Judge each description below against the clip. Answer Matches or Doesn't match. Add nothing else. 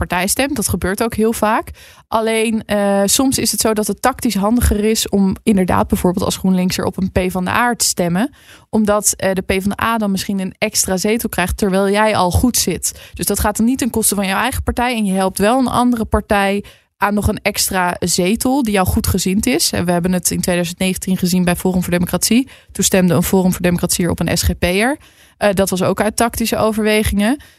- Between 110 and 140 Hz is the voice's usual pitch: Doesn't match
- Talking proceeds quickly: Matches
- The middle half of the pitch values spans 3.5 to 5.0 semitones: Doesn't match